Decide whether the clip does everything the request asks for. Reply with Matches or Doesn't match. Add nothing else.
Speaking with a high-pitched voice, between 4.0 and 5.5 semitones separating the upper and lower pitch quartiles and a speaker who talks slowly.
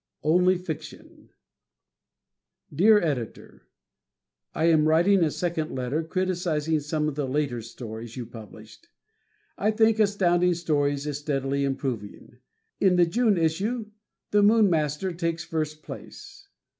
Doesn't match